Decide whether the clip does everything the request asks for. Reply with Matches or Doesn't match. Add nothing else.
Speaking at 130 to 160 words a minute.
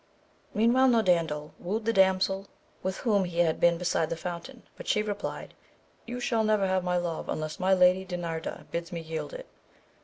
Doesn't match